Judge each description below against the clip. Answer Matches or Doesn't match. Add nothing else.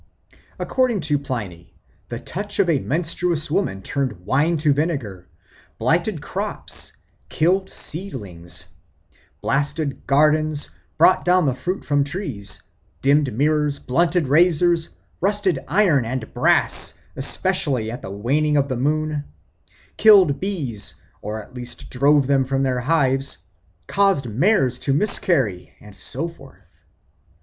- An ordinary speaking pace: Doesn't match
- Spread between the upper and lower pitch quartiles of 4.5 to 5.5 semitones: Matches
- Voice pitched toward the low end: Doesn't match